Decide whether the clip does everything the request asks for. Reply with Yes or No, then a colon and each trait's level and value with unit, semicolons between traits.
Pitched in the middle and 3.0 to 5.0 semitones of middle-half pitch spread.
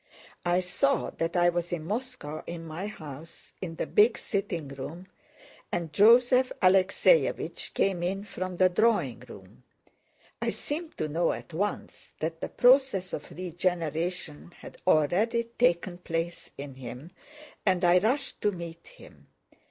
Yes: medium, 175 Hz; average, 4.1 semitones